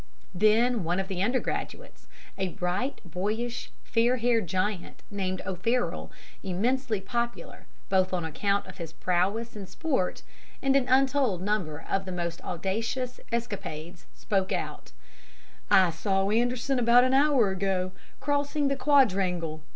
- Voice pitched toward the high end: Yes, high, 205 Hz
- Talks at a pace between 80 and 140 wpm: Yes, slow, 135 wpm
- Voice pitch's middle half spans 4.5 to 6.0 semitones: Yes, average, 5.0 semitones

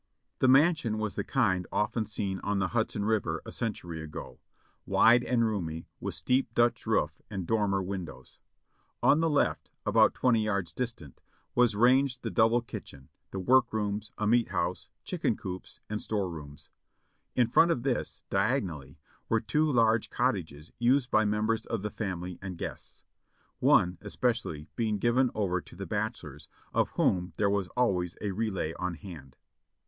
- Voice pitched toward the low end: Yes, low, 105 Hz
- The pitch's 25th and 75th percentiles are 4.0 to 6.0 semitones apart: Yes, average, 4.4 semitones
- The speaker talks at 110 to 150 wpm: No, average, 165 wpm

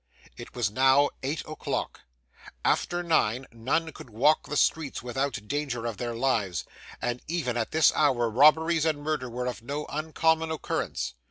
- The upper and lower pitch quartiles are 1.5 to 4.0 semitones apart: No, average, 4.5 semitones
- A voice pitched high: No, low, 135 Hz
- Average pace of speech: Yes, average, 160 wpm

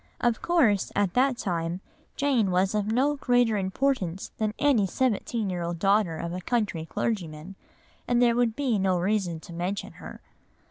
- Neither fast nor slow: Yes, average, 170 wpm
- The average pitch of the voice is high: Yes, high, 205 Hz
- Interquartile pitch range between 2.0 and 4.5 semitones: No, average, 5.1 semitones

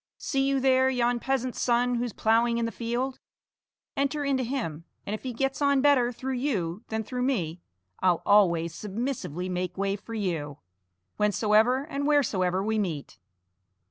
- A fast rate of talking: No, average, 160 wpm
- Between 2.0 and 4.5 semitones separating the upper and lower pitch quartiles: No, wide, 5.4 semitones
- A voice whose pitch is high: Yes, high, 235 Hz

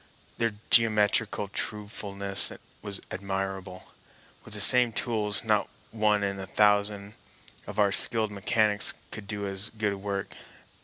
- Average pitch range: No, narrow, 1.4 semitones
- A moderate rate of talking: No, slow, 125 wpm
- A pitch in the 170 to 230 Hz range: No, low, 105 Hz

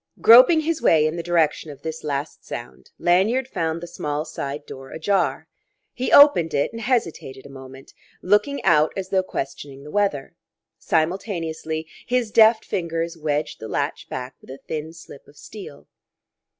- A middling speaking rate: Yes, average, 165 wpm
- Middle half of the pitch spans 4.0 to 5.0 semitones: No, wide, 5.4 semitones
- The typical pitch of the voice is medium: Yes, medium, 160 Hz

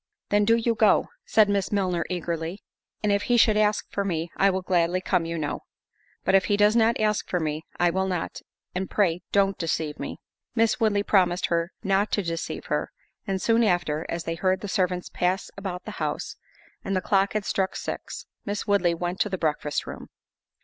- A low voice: No, high, 190 Hz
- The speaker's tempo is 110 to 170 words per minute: No, average, 200 wpm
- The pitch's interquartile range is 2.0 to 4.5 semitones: Yes, average, 2.8 semitones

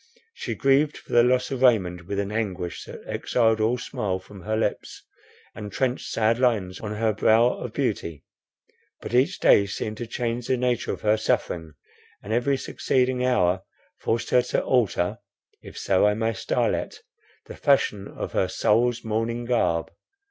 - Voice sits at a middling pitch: No, low, 115 Hz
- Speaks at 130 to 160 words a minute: No, average, 170 wpm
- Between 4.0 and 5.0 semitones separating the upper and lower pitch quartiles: No, average, 3.5 semitones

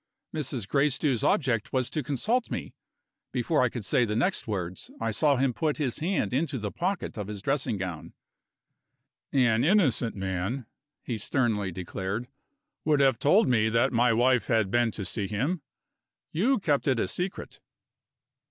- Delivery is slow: No, average, 165 wpm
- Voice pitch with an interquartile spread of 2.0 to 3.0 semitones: No, average, 5.3 semitones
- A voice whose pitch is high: No, low, 125 Hz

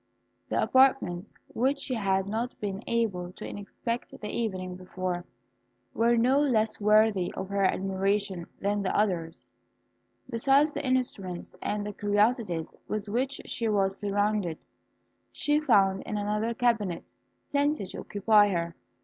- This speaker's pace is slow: Yes, slow, 130 wpm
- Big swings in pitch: No, average, 3.4 semitones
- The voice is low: No, high, 205 Hz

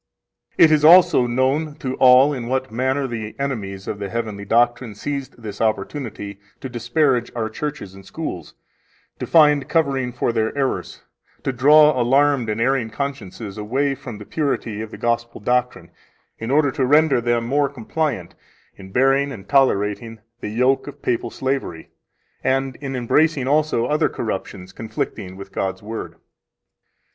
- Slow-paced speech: No, average, 155 wpm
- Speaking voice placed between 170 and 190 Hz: No, low, 125 Hz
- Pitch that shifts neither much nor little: Yes, average, 4.1 semitones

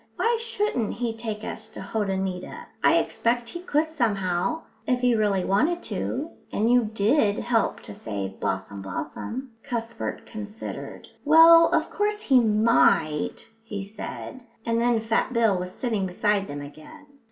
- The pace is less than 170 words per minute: Yes, average, 150 wpm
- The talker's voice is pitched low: No, high, 225 Hz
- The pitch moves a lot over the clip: No, average, 4.8 semitones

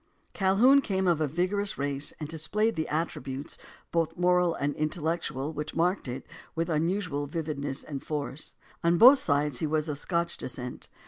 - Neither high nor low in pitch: Yes, medium, 160 Hz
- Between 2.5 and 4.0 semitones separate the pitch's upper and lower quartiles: Yes, average, 3.6 semitones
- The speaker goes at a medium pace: Yes, average, 170 wpm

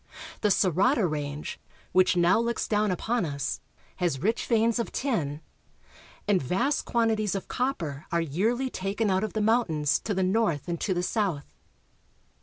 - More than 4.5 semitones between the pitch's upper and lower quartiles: Yes, average, 5.3 semitones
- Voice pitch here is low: No, high, 190 Hz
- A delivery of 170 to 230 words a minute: No, average, 160 wpm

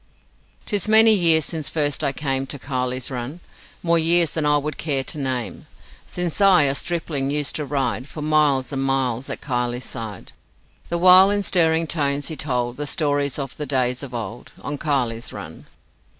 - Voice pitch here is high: No, medium, 145 Hz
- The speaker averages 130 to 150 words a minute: No, average, 180 wpm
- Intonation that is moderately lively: Yes, average, 3.9 semitones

